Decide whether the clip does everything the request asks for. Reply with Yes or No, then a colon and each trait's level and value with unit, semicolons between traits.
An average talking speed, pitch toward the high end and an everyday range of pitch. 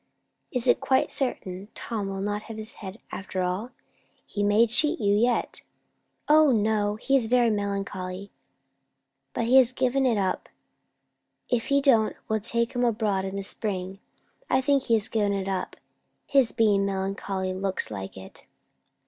Yes: average, 160 wpm; high, 210 Hz; average, 3.8 semitones